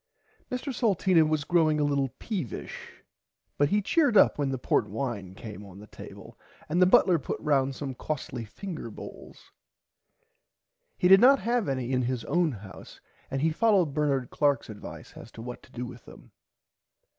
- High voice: No, medium, 145 Hz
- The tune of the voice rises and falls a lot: Yes, wide, 6.6 semitones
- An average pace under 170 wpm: No, average, 175 wpm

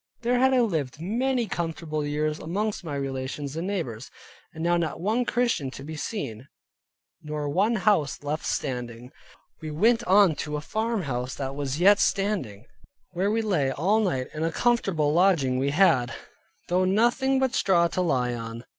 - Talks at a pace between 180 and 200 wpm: No, average, 170 wpm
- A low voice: No, medium, 165 Hz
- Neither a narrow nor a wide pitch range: No, wide, 6.7 semitones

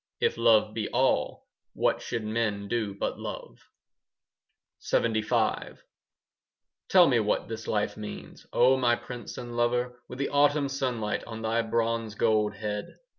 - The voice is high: No, low, 115 Hz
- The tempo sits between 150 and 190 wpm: No, average, 140 wpm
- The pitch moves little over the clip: Yes, narrow, 2.3 semitones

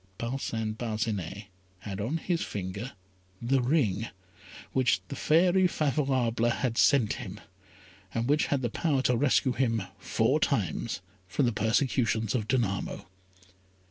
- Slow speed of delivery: Yes, slow, 130 wpm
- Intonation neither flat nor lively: Yes, average, 3.9 semitones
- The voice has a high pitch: No, low, 120 Hz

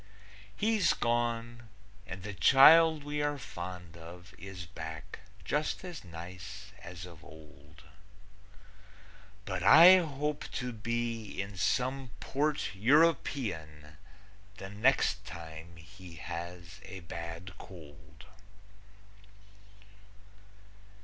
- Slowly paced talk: Yes, slow, 95 wpm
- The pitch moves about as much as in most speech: No, wide, 7.9 semitones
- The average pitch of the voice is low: Yes, very low, 95 Hz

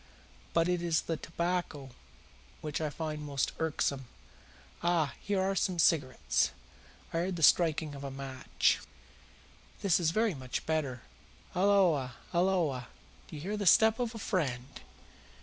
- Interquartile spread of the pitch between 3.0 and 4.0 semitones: No, average, 4.5 semitones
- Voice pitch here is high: No, medium, 160 Hz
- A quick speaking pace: No, average, 145 wpm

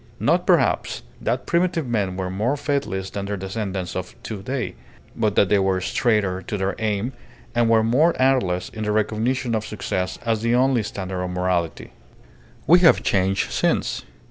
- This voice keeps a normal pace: Yes, average, 170 wpm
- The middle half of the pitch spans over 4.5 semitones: No, average, 4.1 semitones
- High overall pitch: No, low, 105 Hz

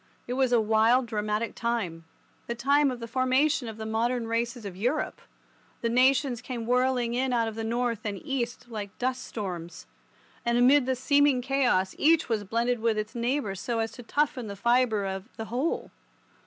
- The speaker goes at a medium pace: Yes, average, 180 wpm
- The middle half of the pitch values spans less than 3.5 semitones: Yes, narrow, 2.6 semitones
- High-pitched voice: Yes, high, 235 Hz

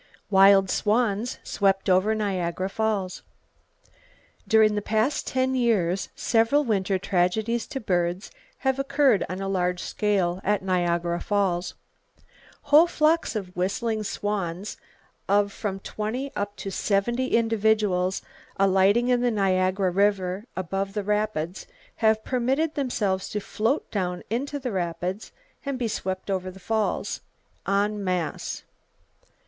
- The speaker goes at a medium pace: No, slow, 125 wpm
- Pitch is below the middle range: No, high, 205 Hz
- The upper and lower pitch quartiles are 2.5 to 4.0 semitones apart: Yes, average, 3.2 semitones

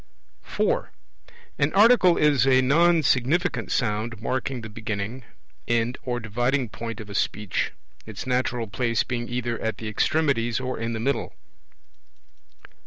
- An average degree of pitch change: Yes, average, 3.1 semitones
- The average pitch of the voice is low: Yes, low, 120 Hz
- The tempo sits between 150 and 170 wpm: No, average, 140 wpm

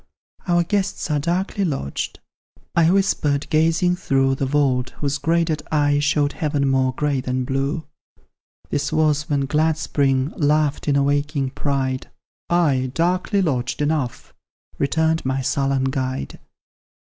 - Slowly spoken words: Yes, slow, 130 wpm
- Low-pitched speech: No, medium, 145 Hz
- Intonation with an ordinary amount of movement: Yes, average, 3.0 semitones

